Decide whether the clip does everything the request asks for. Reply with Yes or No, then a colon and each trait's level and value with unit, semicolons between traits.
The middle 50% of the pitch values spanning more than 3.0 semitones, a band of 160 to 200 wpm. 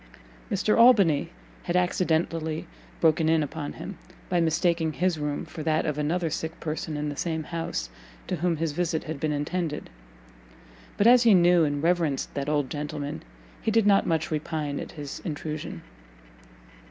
No: narrow, 2.6 semitones; average, 165 wpm